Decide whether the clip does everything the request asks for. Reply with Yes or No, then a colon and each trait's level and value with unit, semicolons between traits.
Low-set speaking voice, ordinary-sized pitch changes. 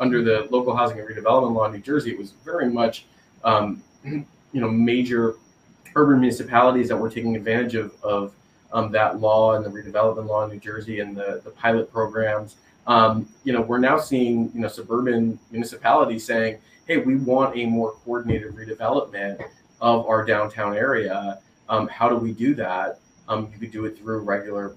No: low, 110 Hz; narrow, 1.9 semitones